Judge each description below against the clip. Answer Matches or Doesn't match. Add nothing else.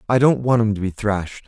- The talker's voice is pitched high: Doesn't match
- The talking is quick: Matches